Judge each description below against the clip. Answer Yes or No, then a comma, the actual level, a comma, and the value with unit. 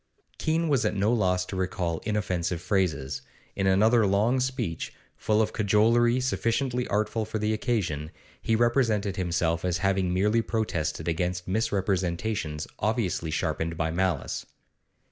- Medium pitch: No, low, 100 Hz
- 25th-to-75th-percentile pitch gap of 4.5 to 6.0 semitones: No, average, 4.1 semitones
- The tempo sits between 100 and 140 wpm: Yes, slow, 135 wpm